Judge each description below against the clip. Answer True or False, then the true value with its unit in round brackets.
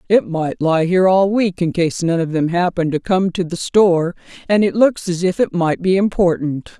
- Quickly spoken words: True (230 wpm)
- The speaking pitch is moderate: True (180 Hz)